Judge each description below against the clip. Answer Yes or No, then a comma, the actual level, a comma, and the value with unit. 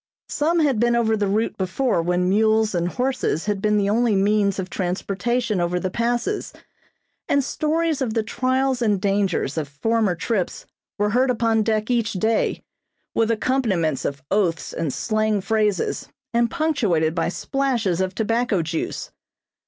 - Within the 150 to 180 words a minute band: Yes, average, 155 wpm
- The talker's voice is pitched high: Yes, high, 215 Hz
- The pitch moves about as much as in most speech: Yes, average, 4.2 semitones